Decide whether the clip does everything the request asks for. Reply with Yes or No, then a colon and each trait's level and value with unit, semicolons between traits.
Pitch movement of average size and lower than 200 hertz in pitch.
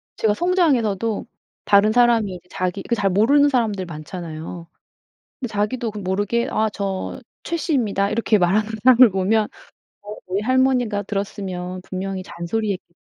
No: average, 3.8 semitones; high, 205 Hz